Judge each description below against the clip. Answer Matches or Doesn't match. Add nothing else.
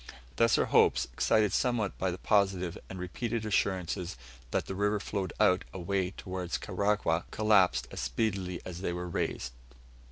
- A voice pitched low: Matches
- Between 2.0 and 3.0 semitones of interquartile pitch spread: Matches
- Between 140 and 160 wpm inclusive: Matches